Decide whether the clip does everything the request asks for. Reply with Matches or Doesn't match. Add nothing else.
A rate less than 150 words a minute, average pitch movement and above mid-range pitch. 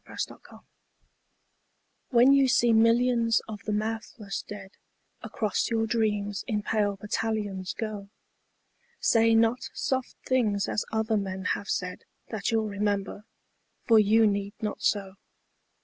Doesn't match